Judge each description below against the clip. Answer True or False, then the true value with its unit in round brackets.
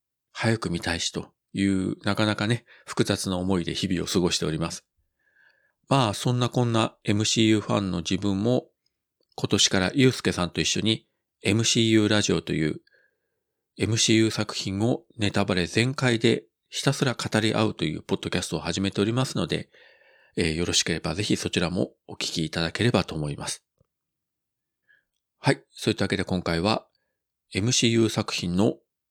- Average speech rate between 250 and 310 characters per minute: False (330 characters per minute)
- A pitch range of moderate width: True (3.6 semitones)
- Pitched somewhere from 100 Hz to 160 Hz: True (105 Hz)